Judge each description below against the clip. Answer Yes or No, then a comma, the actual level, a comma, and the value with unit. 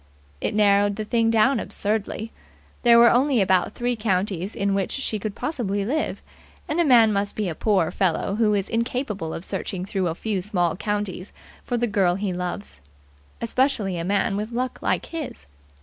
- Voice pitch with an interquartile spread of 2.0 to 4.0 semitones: Yes, average, 3.4 semitones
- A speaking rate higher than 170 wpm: Yes, average, 180 wpm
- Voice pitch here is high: Yes, high, 210 Hz